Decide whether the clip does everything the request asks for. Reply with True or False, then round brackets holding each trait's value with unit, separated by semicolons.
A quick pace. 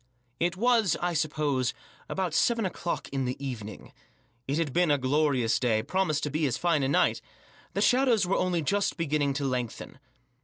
False (185 wpm)